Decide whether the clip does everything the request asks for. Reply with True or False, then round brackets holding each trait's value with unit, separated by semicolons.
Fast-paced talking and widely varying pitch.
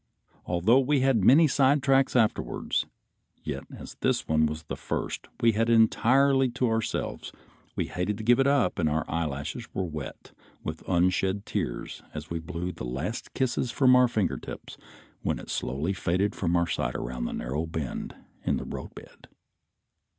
False (165 wpm; 7.6 semitones)